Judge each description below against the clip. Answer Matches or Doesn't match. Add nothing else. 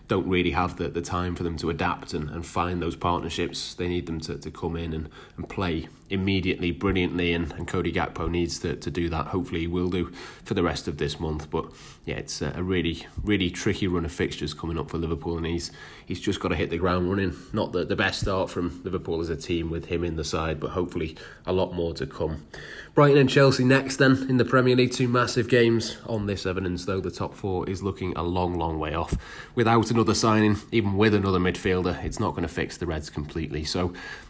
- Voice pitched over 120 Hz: Doesn't match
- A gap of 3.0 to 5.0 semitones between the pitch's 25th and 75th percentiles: Doesn't match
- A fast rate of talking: Matches